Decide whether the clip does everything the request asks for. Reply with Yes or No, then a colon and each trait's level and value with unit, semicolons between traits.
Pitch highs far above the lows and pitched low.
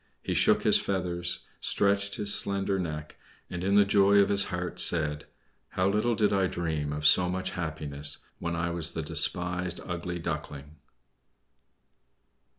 No: average, 3.7 semitones; very low, 90 Hz